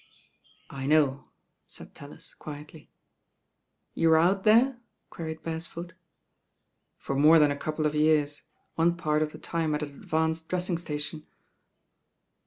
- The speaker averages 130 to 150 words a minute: Yes, slow, 135 wpm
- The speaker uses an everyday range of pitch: No, narrow, 1.9 semitones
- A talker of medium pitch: Yes, medium, 160 Hz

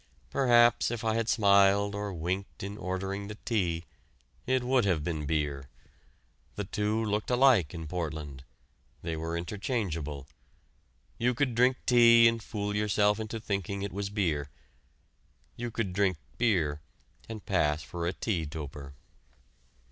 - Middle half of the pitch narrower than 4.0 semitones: No, average, 5.3 semitones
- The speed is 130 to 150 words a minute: Yes, average, 140 wpm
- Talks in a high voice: No, low, 100 Hz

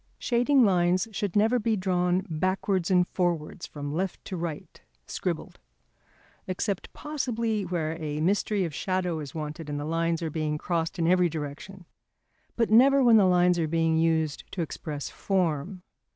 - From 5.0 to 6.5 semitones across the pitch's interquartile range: No, average, 3.4 semitones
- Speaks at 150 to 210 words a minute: Yes, average, 155 wpm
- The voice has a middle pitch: Yes, medium, 180 Hz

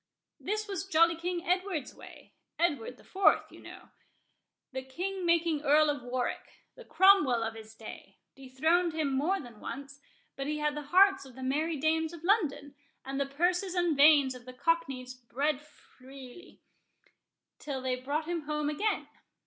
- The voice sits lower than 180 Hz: No, very high, 300 Hz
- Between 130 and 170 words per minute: Yes, average, 155 wpm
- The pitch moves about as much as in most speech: Yes, average, 4.5 semitones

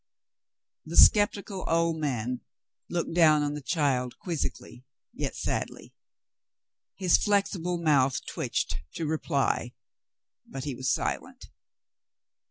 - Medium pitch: Yes, medium, 155 Hz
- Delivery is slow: Yes, slow, 110 wpm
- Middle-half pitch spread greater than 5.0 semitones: No, average, 4.2 semitones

